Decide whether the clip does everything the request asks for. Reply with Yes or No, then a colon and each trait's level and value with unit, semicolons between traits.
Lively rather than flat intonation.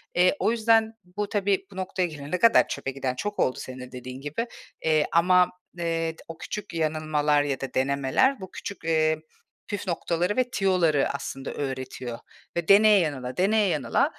Yes: wide, 5.7 semitones